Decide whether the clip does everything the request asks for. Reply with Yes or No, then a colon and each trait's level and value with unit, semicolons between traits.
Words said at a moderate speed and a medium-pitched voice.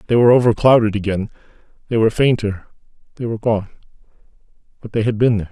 No: average, 165 wpm; low, 110 Hz